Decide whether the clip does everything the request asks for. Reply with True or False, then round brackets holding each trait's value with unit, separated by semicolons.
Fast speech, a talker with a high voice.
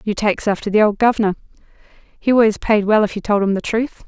True (235 wpm; 210 Hz)